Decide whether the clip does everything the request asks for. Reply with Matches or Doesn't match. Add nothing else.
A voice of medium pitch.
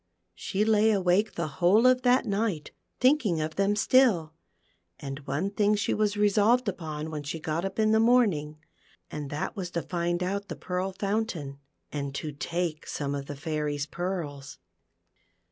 Matches